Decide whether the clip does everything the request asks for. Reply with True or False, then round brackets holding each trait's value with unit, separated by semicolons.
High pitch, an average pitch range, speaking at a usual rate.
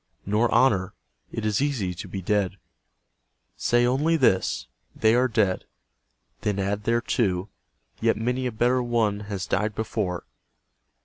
False (110 Hz; 3.4 semitones; 145 wpm)